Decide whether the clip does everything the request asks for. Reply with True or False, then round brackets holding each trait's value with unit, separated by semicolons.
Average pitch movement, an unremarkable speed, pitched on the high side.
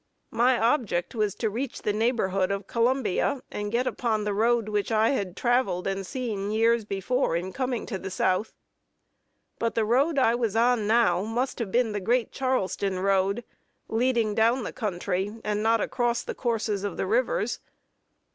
True (3.4 semitones; 175 wpm; 225 Hz)